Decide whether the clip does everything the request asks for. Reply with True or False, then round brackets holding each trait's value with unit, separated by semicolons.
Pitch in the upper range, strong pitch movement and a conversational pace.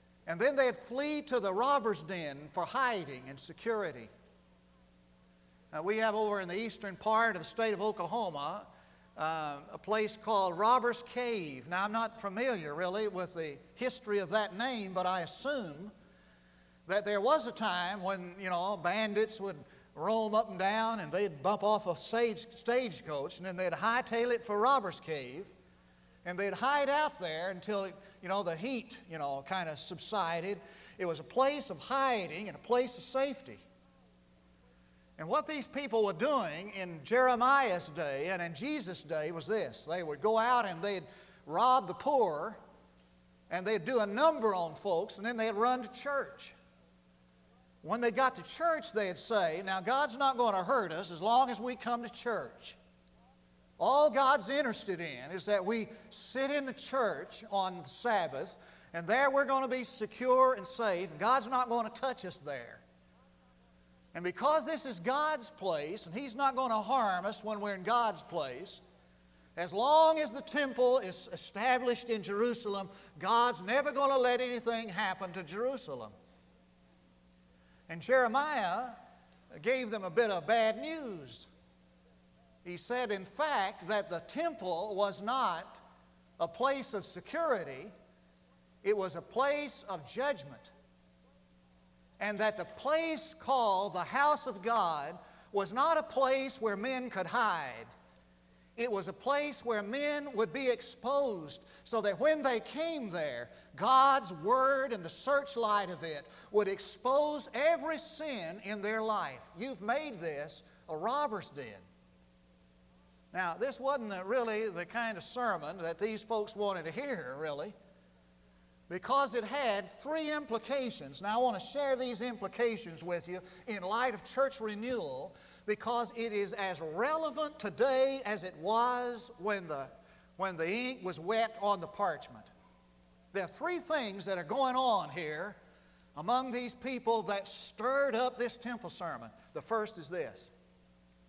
True (210 Hz; 6.7 semitones; 160 wpm)